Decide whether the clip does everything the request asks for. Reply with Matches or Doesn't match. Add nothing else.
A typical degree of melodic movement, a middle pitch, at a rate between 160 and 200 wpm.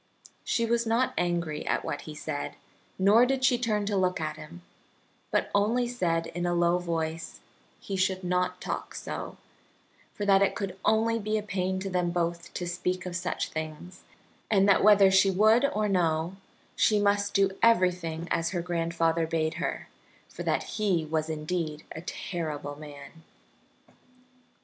Matches